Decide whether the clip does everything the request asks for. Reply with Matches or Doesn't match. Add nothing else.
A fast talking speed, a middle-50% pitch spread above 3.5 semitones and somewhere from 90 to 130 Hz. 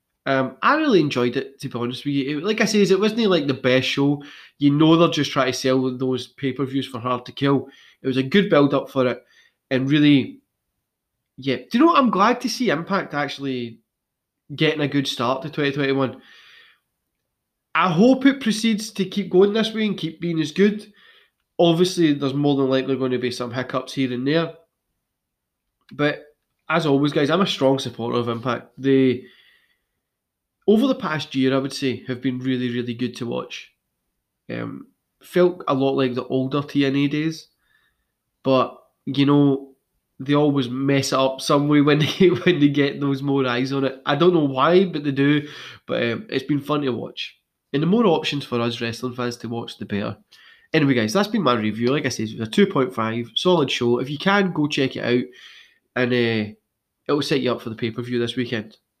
Doesn't match